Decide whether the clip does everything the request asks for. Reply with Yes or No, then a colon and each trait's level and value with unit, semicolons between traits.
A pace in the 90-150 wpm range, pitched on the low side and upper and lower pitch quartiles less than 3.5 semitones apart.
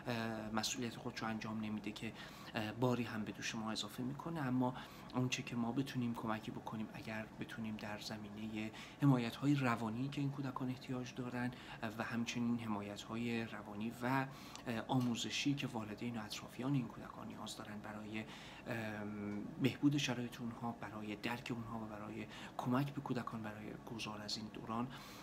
Yes: average, 145 wpm; low, 115 Hz; narrow, 2.6 semitones